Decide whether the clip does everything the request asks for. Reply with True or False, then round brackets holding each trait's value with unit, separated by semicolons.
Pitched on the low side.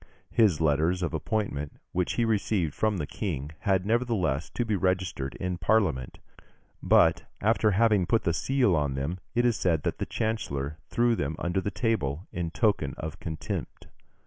True (90 Hz)